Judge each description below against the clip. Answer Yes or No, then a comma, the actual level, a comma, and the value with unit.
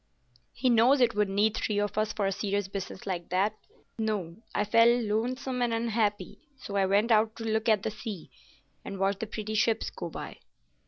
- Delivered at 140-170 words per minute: No, average, 200 wpm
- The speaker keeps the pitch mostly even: Yes, narrow, 2.2 semitones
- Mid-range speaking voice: No, high, 215 Hz